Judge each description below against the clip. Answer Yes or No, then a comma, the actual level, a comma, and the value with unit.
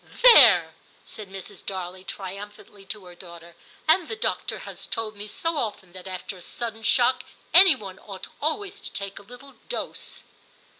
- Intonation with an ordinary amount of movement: No, wide, 5.8 semitones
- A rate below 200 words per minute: Yes, average, 170 wpm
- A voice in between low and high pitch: No, high, 205 Hz